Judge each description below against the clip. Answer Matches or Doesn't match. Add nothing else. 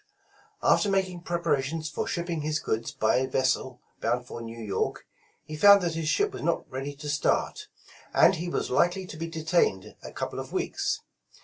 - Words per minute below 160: Doesn't match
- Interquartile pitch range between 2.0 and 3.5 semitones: Doesn't match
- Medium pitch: Matches